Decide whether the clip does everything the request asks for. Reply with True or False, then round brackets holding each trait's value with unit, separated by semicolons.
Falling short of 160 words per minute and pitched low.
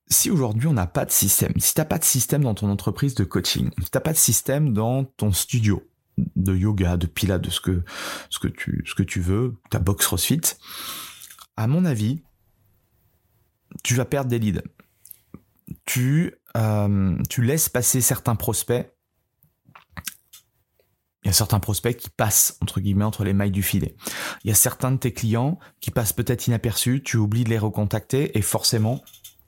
False (185 wpm; 110 Hz)